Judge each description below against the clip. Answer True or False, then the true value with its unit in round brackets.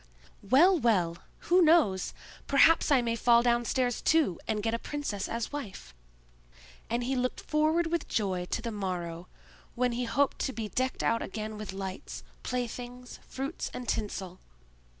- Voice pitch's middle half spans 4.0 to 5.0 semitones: True (4.7 semitones)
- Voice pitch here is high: True (235 Hz)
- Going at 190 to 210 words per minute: False (160 wpm)